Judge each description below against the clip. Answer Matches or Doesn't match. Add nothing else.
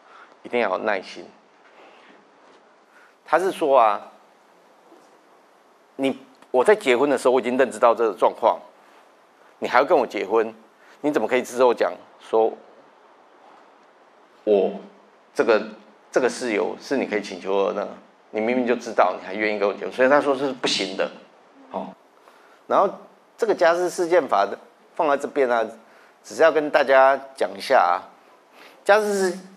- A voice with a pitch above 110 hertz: Matches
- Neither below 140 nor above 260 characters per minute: Matches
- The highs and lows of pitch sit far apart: Matches